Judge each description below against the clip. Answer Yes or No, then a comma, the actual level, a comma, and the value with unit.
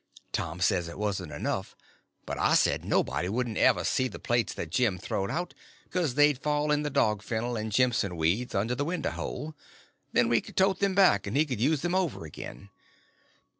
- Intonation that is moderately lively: No, wide, 7.0 semitones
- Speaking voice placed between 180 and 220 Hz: No, low, 120 Hz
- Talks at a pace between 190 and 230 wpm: Yes, average, 195 wpm